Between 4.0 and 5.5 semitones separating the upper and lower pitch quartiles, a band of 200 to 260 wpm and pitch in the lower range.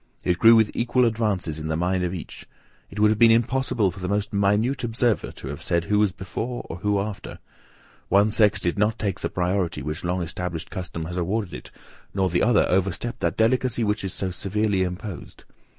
No: average, 3.6 semitones; fast, 205 wpm; low, 100 Hz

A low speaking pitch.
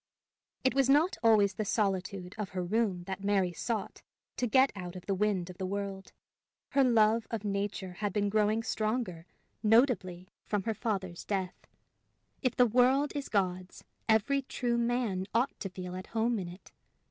No: high, 205 Hz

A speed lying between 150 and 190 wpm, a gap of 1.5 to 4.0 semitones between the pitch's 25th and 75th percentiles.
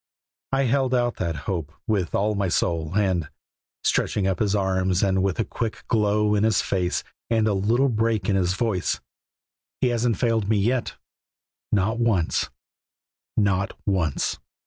Yes: average, 155 wpm; average, 3.3 semitones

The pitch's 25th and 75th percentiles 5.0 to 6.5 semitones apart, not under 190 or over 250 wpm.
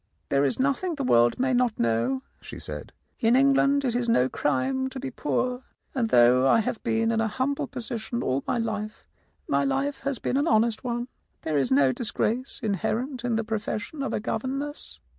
No: average, 3.8 semitones; average, 200 wpm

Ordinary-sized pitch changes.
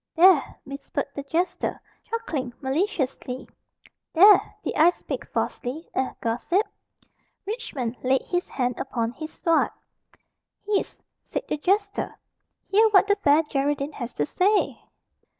No: wide, 6.5 semitones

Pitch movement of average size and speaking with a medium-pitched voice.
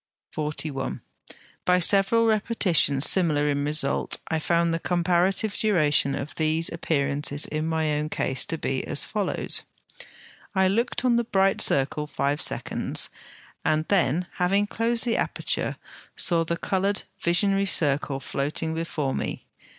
Yes: average, 4.7 semitones; medium, 165 Hz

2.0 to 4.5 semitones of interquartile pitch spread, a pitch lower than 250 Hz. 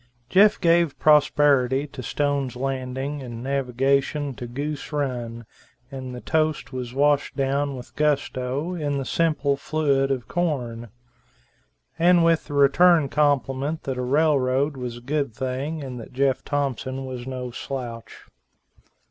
Yes: narrow, 2.5 semitones; low, 135 Hz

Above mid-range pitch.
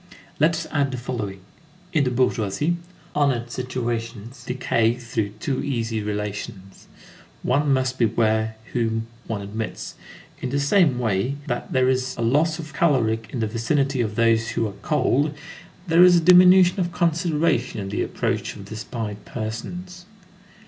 No: low, 125 Hz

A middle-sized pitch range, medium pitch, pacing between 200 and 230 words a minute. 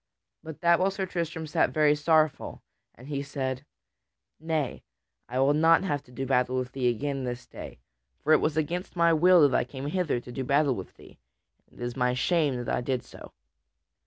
Yes: average, 3.9 semitones; medium, 145 Hz; fast, 205 wpm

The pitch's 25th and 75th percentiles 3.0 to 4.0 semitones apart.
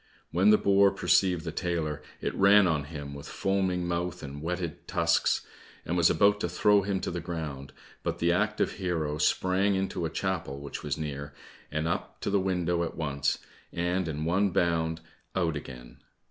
Yes: average, 3.5 semitones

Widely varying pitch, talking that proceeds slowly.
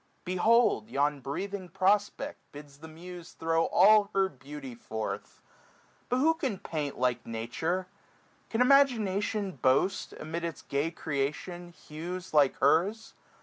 Yes: wide, 5.8 semitones; slow, 130 wpm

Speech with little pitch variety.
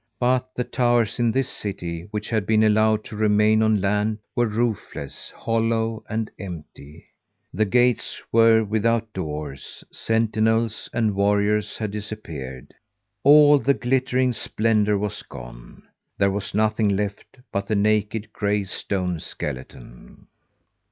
Yes: narrow, 2.2 semitones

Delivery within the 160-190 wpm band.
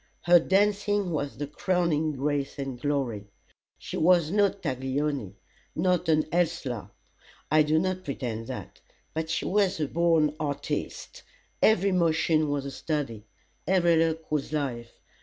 No: average, 140 wpm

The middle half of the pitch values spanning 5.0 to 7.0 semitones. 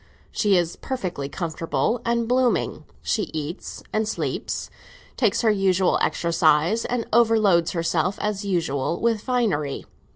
Yes: wide, 5.4 semitones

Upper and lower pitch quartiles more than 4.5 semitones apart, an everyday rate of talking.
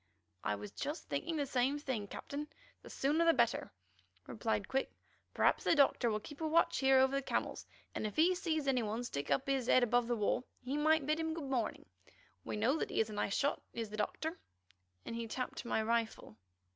No: average, 5.0 semitones; fast, 210 wpm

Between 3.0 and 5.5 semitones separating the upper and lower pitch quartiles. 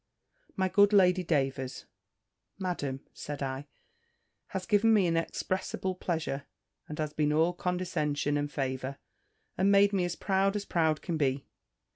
Yes: average, 4.5 semitones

